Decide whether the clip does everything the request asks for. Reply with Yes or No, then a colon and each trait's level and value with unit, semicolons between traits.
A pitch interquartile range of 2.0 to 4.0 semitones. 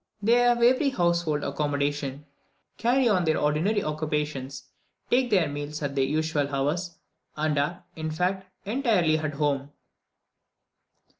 No: average, 4.8 semitones